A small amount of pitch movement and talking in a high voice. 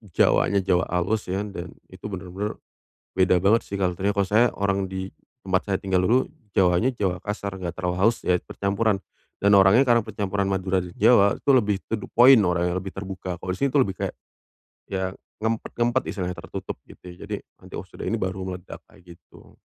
No: narrow, 2.1 semitones; very low, 95 Hz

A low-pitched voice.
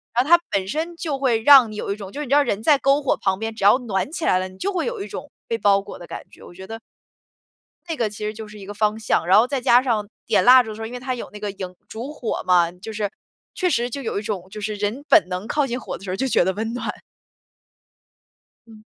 No: high, 220 Hz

